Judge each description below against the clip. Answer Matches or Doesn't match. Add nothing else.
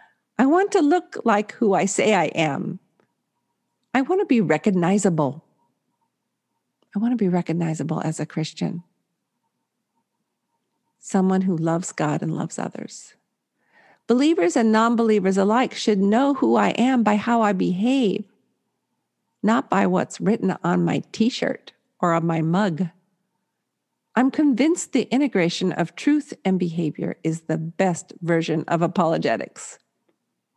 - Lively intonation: Matches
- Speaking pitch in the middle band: Doesn't match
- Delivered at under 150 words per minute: Matches